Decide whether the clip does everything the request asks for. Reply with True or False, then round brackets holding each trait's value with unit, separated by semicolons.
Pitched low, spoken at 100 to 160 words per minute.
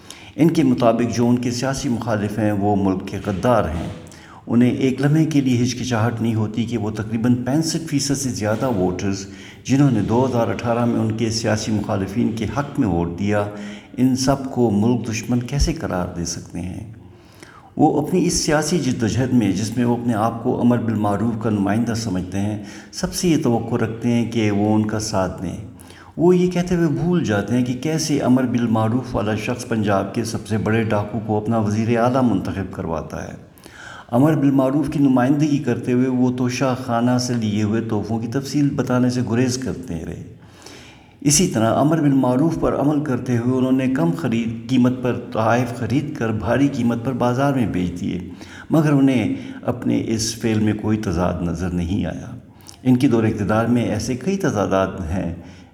False (115 Hz; 190 wpm)